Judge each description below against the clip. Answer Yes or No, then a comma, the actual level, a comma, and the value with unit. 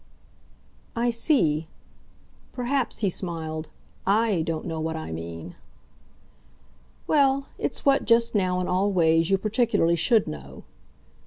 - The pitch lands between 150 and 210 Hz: Yes, medium, 185 Hz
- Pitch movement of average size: No, wide, 6.4 semitones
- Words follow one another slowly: Yes, slow, 120 wpm